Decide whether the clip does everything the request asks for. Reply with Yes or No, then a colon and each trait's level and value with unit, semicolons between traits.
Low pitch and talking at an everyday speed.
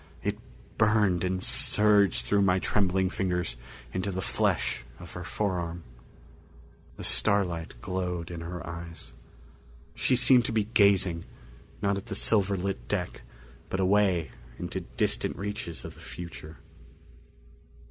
No: very low, 95 Hz; slow, 130 wpm